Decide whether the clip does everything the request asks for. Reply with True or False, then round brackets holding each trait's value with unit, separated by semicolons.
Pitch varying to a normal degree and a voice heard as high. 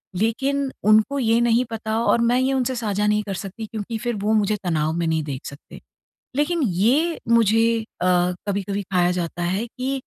True (4.1 semitones; 220 Hz)